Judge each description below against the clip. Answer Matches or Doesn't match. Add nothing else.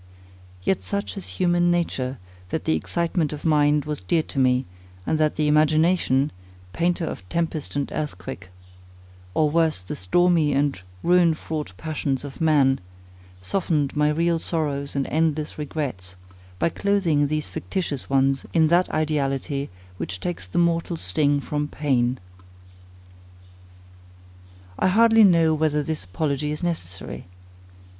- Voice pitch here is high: Doesn't match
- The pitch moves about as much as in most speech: Matches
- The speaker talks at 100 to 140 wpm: Matches